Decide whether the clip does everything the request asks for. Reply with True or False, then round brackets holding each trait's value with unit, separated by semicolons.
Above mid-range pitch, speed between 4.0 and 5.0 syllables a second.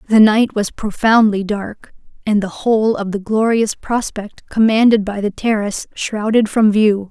True (215 Hz; 4.4 syllables/s)